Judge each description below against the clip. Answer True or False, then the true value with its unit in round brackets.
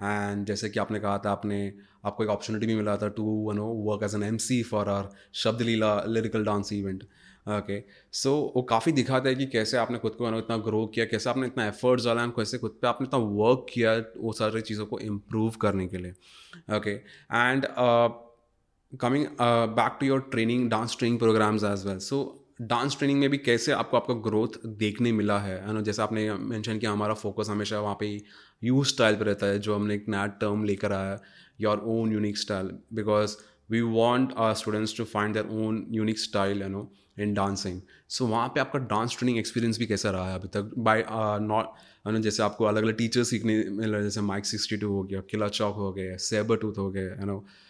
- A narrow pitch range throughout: True (2.1 semitones)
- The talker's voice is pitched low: True (110 Hz)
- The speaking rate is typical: False (215 wpm)